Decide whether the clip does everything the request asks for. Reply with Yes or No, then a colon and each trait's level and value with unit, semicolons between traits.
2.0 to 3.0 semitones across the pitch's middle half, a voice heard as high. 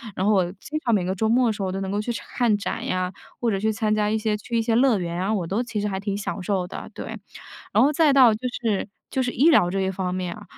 No: average, 3.5 semitones; high, 210 Hz